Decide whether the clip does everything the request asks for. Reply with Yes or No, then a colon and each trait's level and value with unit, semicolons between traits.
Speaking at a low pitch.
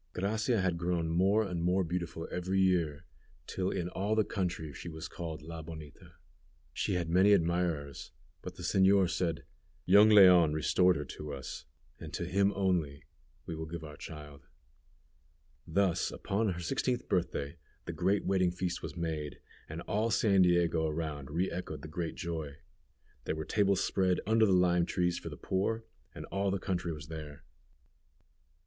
Yes: very low, 90 Hz